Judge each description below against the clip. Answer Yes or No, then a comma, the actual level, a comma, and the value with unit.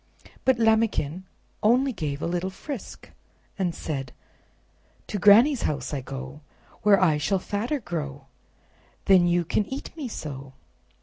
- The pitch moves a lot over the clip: Yes, wide, 7.0 semitones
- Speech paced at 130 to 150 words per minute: Yes, slow, 135 wpm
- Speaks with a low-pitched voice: No, medium, 185 Hz